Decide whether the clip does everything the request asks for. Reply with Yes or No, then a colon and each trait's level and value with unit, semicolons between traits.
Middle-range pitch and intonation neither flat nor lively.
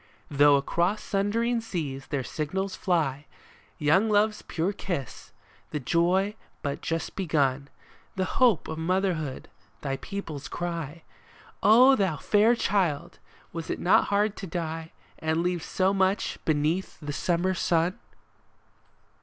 Yes: medium, 175 Hz; average, 4.5 semitones